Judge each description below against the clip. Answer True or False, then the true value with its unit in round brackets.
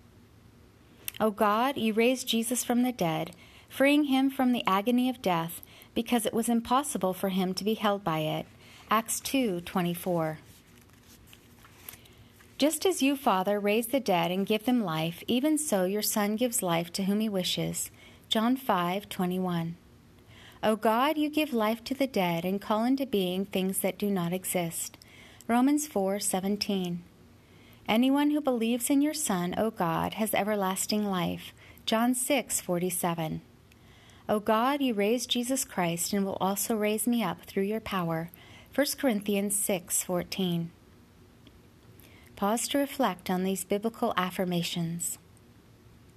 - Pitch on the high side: True (195 Hz)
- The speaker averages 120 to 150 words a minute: True (145 wpm)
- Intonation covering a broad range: True (5.8 semitones)